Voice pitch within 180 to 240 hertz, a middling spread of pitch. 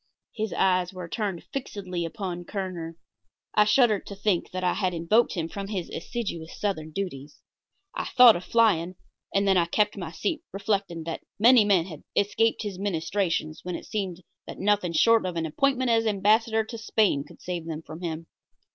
Yes: high, 190 Hz; average, 3.9 semitones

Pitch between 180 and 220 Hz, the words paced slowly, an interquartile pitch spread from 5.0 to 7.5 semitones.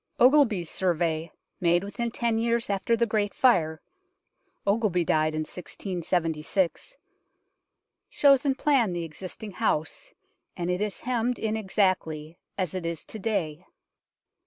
Yes: high, 190 Hz; slow, 130 wpm; wide, 5.4 semitones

